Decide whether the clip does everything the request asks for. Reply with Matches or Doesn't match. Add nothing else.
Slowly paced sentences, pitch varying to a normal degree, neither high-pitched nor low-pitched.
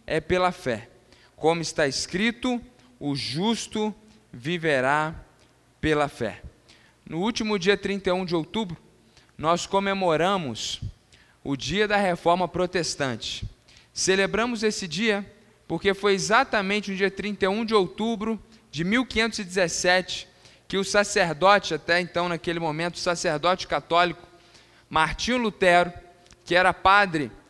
Matches